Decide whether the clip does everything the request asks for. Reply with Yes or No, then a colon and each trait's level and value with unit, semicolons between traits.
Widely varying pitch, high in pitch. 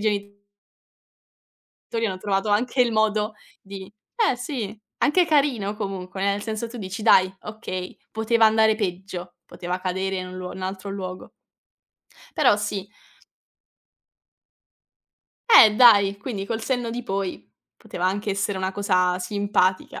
No: average, 2.7 semitones; high, 200 Hz